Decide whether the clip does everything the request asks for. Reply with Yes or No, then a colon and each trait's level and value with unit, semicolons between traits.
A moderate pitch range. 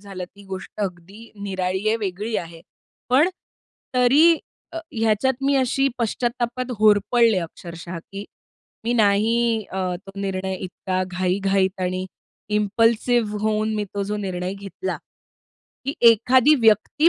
Yes: average, 3.9 semitones